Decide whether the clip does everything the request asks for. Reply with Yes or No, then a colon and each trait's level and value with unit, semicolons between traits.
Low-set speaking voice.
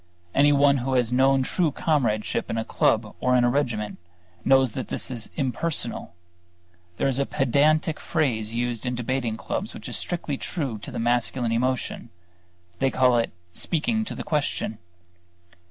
Yes: low, 130 Hz